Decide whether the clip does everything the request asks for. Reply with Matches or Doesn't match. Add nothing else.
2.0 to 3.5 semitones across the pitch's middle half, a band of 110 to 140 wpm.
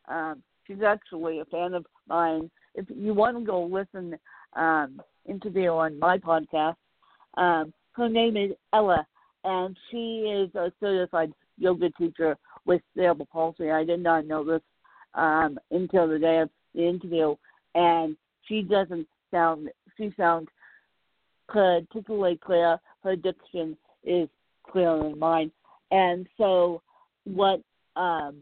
Matches